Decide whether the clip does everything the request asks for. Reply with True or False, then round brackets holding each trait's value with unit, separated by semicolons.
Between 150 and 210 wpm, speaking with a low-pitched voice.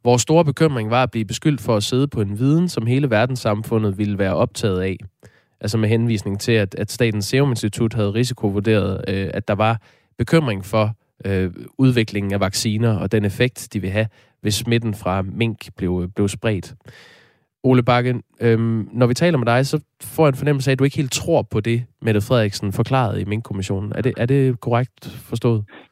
True (185 wpm; 115 Hz)